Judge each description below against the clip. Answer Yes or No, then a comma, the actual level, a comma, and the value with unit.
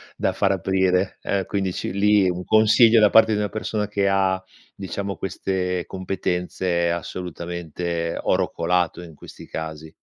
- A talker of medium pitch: No, very low, 95 Hz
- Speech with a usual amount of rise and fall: No, narrow, 2.3 semitones